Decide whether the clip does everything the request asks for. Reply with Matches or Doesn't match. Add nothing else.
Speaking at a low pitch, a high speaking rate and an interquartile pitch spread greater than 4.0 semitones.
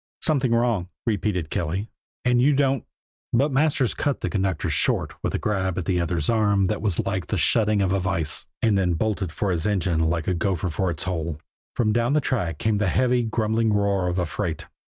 Matches